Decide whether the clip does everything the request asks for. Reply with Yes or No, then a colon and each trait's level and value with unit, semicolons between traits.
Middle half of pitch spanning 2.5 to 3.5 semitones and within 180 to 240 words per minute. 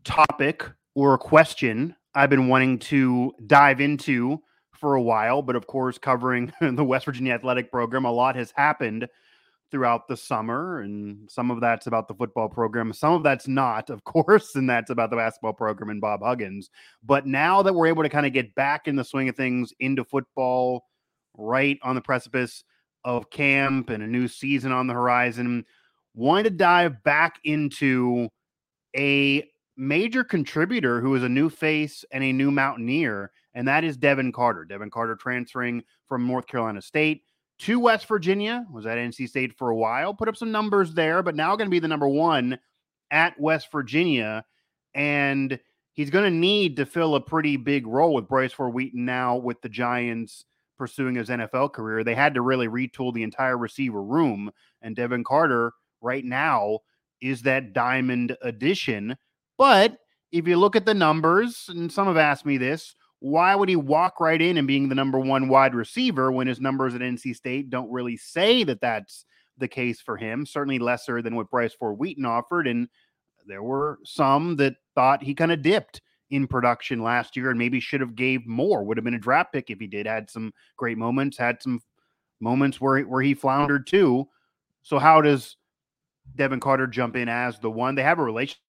Yes: average, 3.2 semitones; average, 190 wpm